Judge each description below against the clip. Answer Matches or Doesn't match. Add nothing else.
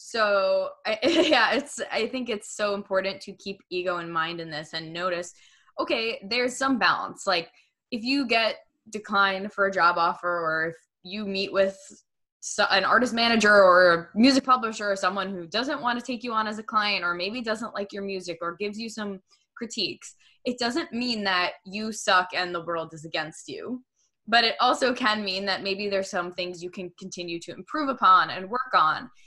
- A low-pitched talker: Doesn't match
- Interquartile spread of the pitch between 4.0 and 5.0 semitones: Matches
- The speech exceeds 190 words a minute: Matches